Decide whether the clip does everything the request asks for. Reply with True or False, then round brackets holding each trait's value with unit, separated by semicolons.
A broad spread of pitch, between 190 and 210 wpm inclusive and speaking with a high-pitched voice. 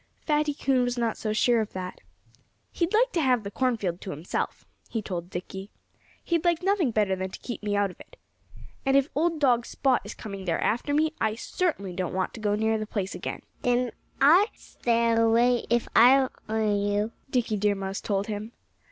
False (4.8 semitones; 200 wpm; 230 Hz)